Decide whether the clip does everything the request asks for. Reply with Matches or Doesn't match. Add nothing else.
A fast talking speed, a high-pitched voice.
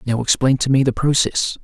Doesn't match